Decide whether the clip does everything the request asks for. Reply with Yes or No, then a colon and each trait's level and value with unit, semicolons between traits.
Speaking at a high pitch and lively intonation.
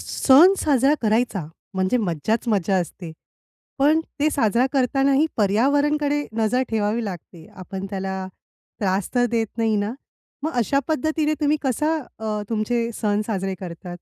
Yes: high, 225 Hz; wide, 6.1 semitones